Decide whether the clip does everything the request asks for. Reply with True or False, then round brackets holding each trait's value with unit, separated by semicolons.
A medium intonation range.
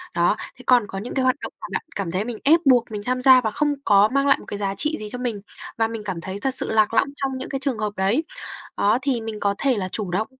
True (4.1 semitones)